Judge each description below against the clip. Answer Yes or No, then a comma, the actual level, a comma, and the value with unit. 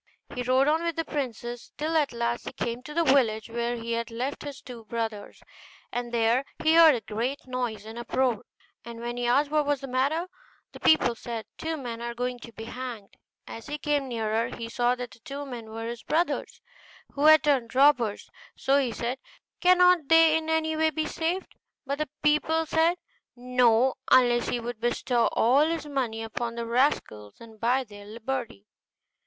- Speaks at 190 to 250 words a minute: Yes, average, 195 wpm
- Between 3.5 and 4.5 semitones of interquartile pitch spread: Yes, average, 4.1 semitones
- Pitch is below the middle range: No, very high, 250 Hz